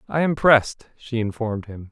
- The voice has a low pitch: Yes, low, 120 Hz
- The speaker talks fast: No, average, 190 wpm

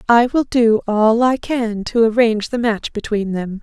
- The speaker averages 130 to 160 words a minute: No, average, 200 wpm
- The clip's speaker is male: No, female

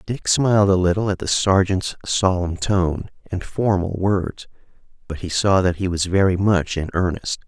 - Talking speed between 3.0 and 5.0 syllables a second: Yes, 4.6 syllables/s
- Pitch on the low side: Yes, very low, 95 Hz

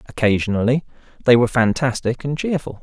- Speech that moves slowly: Yes, slow, 125 wpm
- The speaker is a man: Yes, male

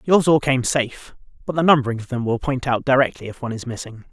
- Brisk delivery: Yes, fast, 250 wpm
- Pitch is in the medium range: No, low, 130 Hz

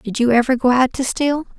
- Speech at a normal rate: No, fast, 265 wpm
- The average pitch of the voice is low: No, very high, 255 Hz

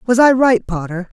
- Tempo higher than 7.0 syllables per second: No, 5.1 syllables/s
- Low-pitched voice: No, high, 220 Hz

